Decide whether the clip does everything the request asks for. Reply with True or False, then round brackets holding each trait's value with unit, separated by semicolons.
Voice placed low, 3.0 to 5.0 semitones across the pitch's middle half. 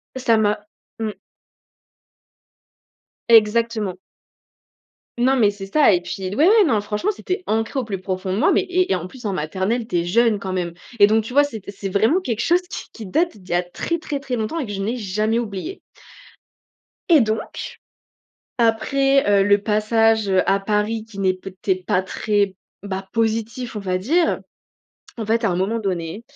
False (215 Hz; 3.7 semitones)